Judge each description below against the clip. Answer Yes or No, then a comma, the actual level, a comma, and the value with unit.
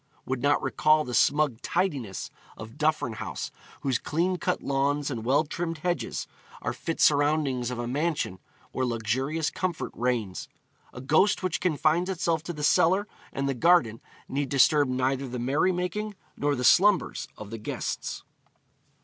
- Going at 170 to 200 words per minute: No, average, 155 wpm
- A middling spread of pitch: Yes, average, 4.8 semitones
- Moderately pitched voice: Yes, medium, 145 Hz